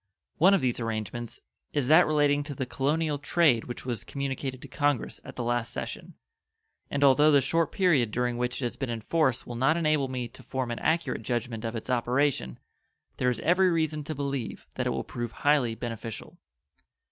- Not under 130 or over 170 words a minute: No, average, 195 wpm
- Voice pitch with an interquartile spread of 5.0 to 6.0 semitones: No, average, 3.7 semitones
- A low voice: Yes, low, 130 Hz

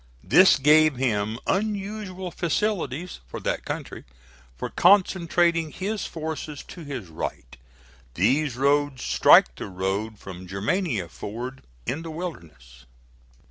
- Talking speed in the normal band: No, slow, 115 wpm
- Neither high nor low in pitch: Yes, medium, 145 Hz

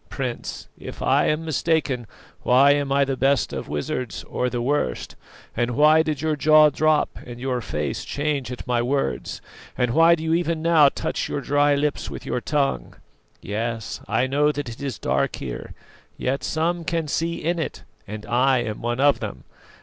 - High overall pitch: No, medium, 140 Hz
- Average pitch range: Yes, average, 4.1 semitones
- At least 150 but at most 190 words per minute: Yes, average, 185 wpm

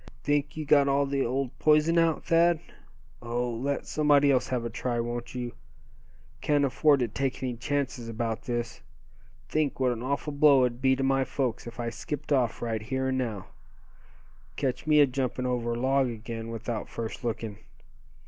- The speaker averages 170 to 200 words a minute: Yes, average, 180 wpm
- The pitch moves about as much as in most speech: Yes, average, 3.0 semitones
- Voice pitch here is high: No, low, 130 Hz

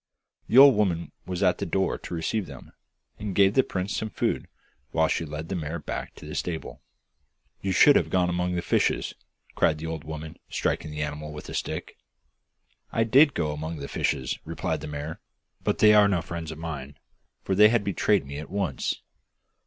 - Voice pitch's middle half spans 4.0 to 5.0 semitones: Yes, average, 4.7 semitones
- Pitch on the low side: Yes, very low, 85 Hz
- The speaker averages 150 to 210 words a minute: Yes, average, 195 wpm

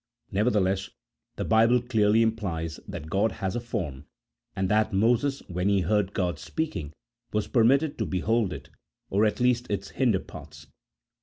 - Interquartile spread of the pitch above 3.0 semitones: Yes, average, 3.8 semitones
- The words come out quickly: No, average, 155 wpm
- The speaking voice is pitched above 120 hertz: No, low, 105 Hz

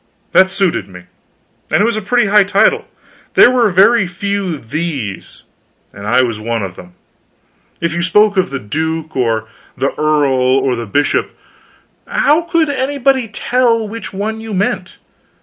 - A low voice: No, medium, 185 Hz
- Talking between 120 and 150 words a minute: No, average, 160 wpm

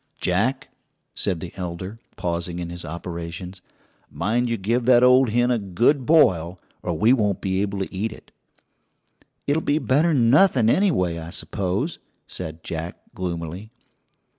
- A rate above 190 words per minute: No, average, 145 wpm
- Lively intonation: Yes, wide, 6.0 semitones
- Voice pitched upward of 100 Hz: No, very low, 95 Hz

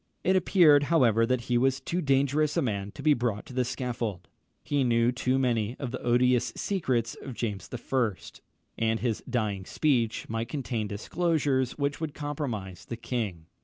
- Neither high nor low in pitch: No, low, 125 Hz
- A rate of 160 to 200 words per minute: Yes, average, 170 wpm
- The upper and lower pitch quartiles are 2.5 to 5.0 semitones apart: Yes, average, 3.7 semitones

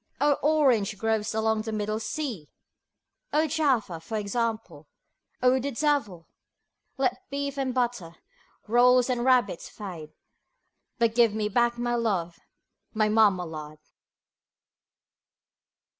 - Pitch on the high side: Yes, high, 225 Hz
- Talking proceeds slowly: Yes, slow, 115 wpm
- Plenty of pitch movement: No, average, 3.7 semitones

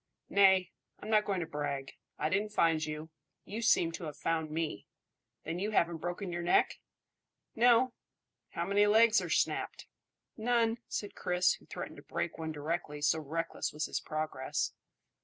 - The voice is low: No, medium, 170 Hz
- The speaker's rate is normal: Yes, average, 165 wpm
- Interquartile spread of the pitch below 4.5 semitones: No, average, 4.8 semitones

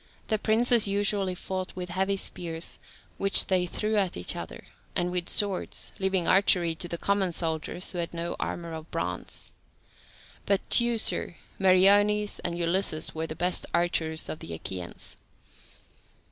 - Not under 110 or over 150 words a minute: Yes, average, 145 wpm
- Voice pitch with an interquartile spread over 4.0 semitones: No, average, 2.9 semitones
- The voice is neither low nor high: Yes, medium, 180 Hz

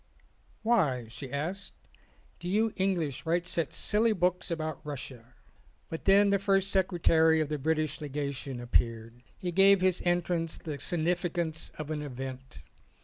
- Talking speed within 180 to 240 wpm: No, average, 150 wpm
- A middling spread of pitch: Yes, average, 4.6 semitones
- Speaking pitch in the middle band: Yes, medium, 160 Hz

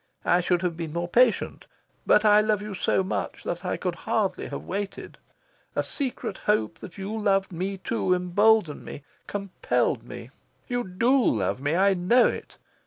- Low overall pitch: No, high, 195 Hz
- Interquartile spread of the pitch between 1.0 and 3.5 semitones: Yes, average, 3.2 semitones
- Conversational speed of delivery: Yes, average, 175 wpm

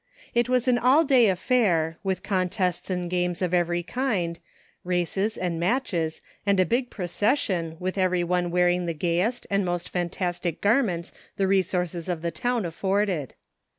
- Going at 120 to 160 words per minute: Yes, average, 150 wpm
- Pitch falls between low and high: Yes, medium, 180 Hz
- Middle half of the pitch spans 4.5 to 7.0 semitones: No, average, 3.1 semitones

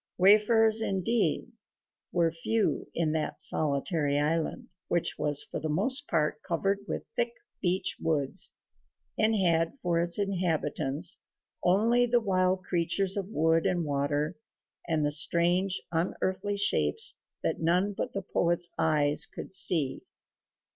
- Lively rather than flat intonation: No, average, 3.9 semitones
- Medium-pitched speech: Yes, medium, 175 Hz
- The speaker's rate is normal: No, slow, 130 wpm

